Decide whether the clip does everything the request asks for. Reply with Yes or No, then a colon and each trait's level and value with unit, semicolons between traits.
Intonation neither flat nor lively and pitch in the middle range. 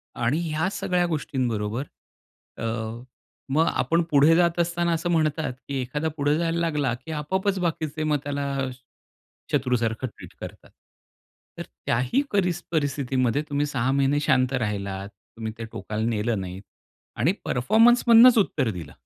No: wide, 5.7 semitones; medium, 145 Hz